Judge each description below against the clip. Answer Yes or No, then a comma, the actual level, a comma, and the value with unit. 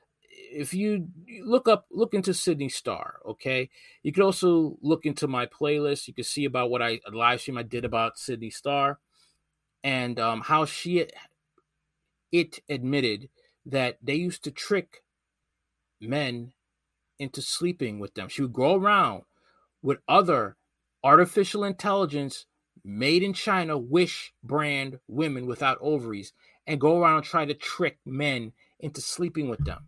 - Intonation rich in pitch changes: Yes, wide, 5.8 semitones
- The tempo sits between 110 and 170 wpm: Yes, average, 150 wpm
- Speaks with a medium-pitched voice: Yes, medium, 145 Hz